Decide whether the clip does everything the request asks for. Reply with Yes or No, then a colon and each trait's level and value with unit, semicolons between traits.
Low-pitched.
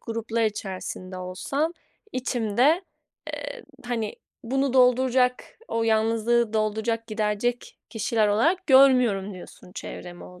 No: high, 230 Hz